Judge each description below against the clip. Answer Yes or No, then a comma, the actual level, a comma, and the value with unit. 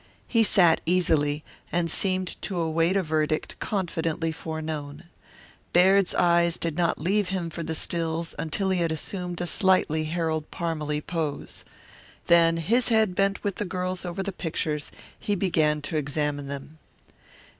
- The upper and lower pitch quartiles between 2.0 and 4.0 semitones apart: Yes, average, 2.7 semitones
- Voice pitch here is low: No, medium, 165 Hz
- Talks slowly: No, average, 150 wpm